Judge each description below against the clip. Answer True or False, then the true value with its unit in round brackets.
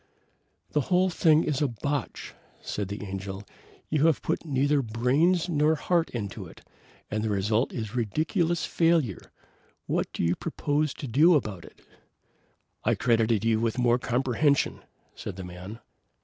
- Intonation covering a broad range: True (6.2 semitones)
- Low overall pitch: True (125 Hz)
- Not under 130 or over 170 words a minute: True (150 wpm)